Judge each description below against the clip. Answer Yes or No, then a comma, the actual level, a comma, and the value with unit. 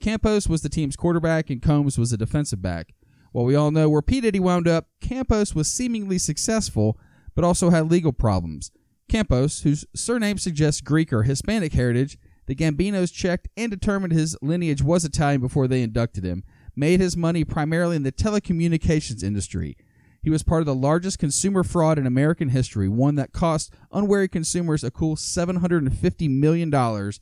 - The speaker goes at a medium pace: Yes, average, 170 wpm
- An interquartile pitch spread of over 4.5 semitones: Yes, average, 5.2 semitones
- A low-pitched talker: No, medium, 155 Hz